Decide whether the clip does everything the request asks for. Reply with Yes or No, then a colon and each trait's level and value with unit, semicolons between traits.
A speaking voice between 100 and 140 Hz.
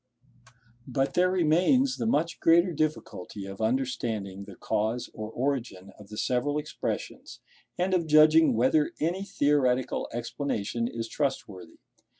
Yes: low, 135 Hz